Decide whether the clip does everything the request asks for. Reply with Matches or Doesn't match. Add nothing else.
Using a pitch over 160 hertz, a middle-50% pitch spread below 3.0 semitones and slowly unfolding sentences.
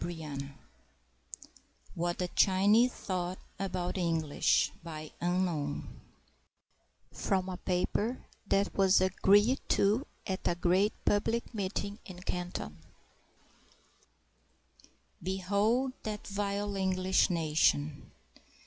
Matches